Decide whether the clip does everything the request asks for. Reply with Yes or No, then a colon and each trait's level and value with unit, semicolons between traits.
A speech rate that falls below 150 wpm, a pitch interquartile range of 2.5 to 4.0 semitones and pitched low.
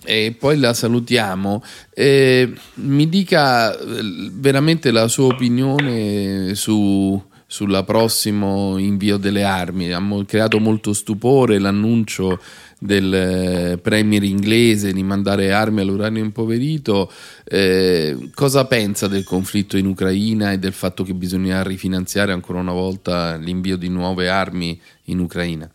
Yes: average, 120 wpm; average, 3.1 semitones; low, 100 Hz